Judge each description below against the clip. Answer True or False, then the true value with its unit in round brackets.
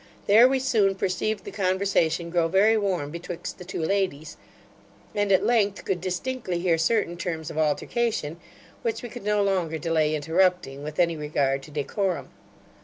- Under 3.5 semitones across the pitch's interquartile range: False (4.1 semitones)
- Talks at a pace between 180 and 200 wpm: False (165 wpm)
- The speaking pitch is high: False (180 Hz)